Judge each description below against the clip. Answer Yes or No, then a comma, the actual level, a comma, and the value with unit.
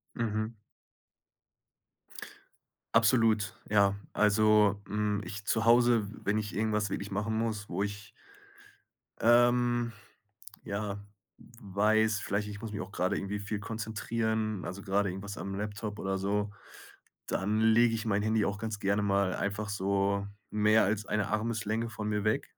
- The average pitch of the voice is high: No, low, 105 Hz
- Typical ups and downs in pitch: No, narrow, 1.6 semitones